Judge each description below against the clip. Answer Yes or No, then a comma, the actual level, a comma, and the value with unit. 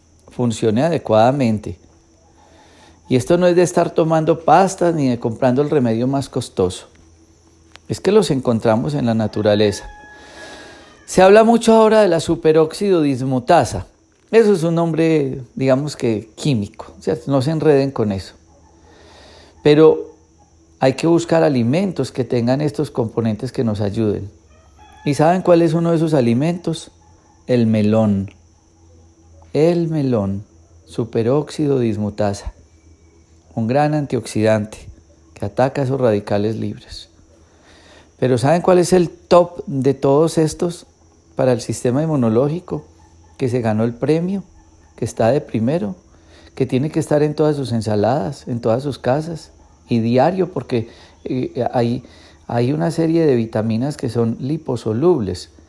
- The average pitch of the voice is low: Yes, low, 120 Hz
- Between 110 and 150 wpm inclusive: Yes, average, 135 wpm